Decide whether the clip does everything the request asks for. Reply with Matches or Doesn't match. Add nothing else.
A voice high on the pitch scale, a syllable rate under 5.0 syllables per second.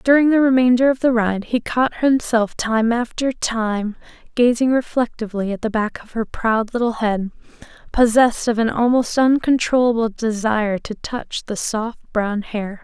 Matches